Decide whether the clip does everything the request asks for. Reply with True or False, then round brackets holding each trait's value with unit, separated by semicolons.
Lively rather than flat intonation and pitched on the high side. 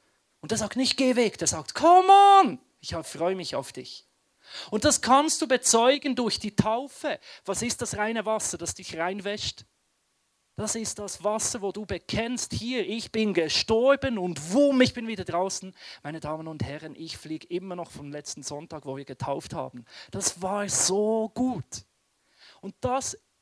True (6.5 semitones; 205 Hz)